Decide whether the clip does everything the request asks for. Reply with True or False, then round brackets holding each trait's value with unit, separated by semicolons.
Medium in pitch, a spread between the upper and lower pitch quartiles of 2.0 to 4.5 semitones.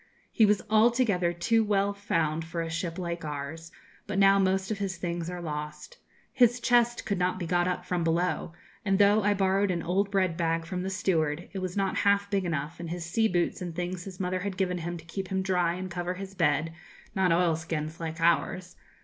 True (180 Hz; 2.7 semitones)